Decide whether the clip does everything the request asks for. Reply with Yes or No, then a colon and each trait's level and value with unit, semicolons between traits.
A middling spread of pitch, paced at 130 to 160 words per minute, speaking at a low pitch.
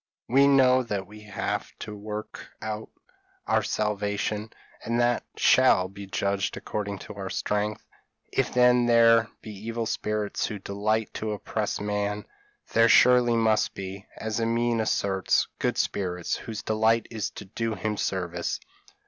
No: narrow, 2.2 semitones; average, 150 wpm; low, 105 Hz